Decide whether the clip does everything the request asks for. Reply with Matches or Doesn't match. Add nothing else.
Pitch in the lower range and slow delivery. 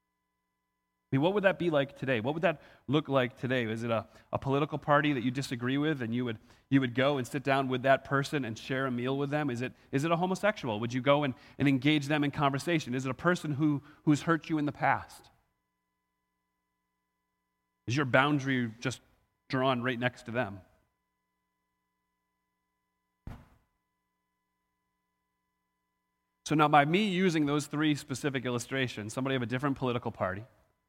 Doesn't match